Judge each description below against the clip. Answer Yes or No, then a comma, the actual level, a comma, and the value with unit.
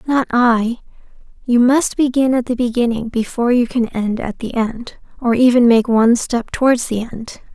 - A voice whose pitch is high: Yes, high, 240 Hz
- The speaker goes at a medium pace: Yes, average, 185 wpm